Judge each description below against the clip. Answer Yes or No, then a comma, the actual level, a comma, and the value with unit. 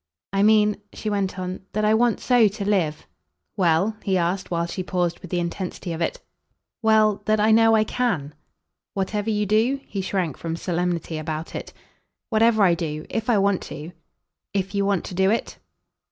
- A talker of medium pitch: No, high, 195 Hz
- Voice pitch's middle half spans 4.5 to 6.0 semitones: No, average, 3.7 semitones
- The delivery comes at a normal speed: Yes, average, 190 wpm